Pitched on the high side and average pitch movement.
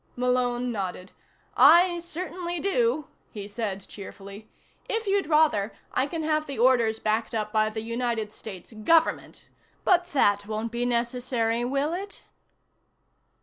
No: high, 240 Hz; wide, 6.1 semitones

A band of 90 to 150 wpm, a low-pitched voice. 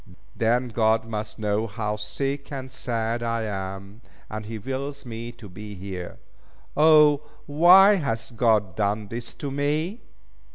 Yes: average, 140 wpm; low, 115 Hz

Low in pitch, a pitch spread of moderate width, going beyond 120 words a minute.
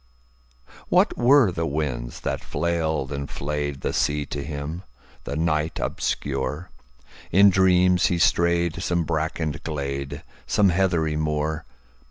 No: very low, 80 Hz; average, 3.1 semitones; slow, 110 wpm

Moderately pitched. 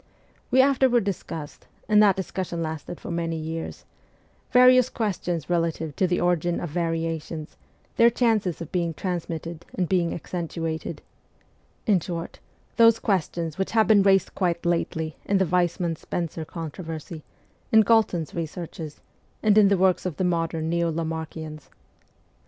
Yes: medium, 170 Hz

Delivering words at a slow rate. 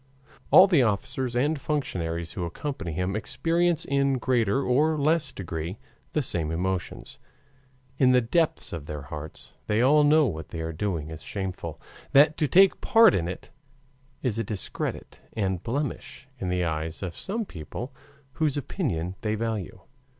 No: average, 160 wpm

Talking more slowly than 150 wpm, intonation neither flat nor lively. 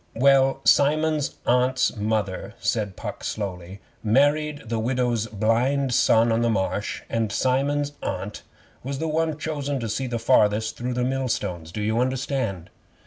Yes: average, 140 wpm; average, 4.2 semitones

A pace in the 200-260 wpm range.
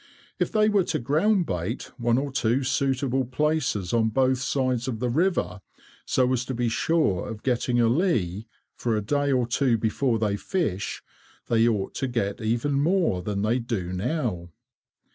No: average, 170 wpm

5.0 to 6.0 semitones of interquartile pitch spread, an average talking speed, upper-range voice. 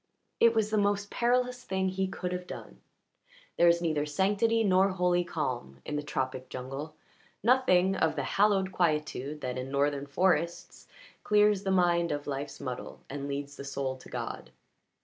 No: wide, 5.4 semitones; average, 170 wpm; medium, 170 Hz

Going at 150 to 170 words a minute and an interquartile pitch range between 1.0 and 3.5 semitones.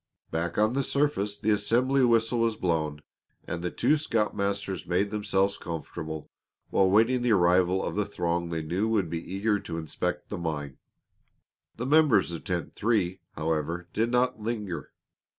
No: average, 160 wpm; average, 4.9 semitones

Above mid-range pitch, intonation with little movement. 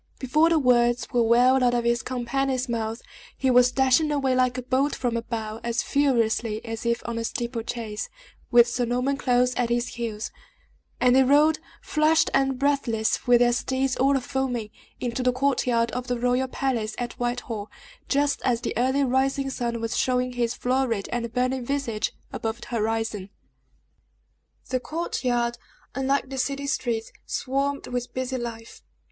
Yes: very high, 250 Hz; narrow, 2.1 semitones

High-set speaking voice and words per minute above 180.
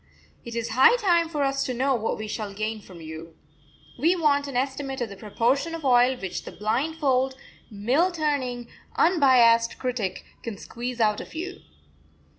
No: very high, 250 Hz; average, 170 wpm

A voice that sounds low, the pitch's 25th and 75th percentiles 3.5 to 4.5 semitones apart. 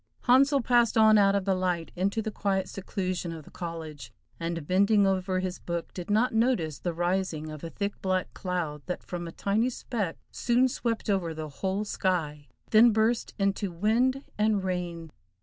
No: high, 190 Hz; average, 4.1 semitones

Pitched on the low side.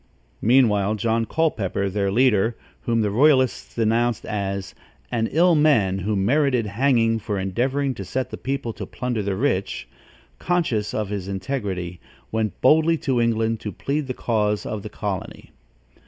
Yes: low, 115 Hz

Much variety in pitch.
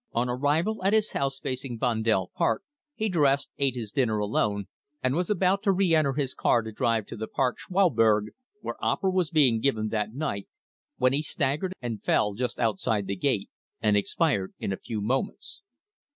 Yes: wide, 6.0 semitones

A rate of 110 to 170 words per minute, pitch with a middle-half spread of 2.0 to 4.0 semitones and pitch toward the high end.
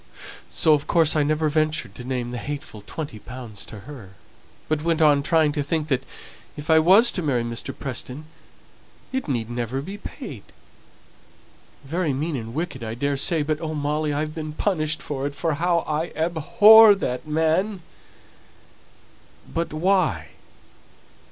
No: average, 155 wpm; average, 3.5 semitones; medium, 150 Hz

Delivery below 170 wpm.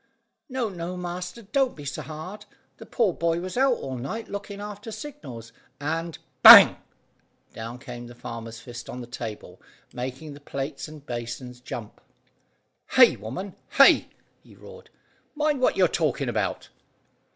Yes: average, 150 wpm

